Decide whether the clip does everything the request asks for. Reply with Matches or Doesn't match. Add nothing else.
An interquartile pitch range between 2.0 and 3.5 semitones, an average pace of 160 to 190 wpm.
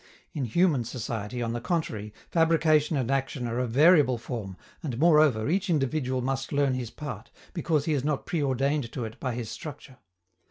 Doesn't match